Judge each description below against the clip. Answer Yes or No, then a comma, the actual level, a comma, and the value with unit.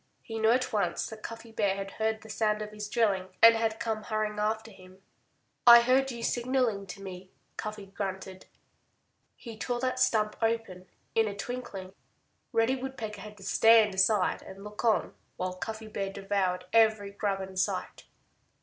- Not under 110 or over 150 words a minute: No, average, 170 wpm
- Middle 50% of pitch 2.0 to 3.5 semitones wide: Yes, narrow, 2.5 semitones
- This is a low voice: No, high, 215 Hz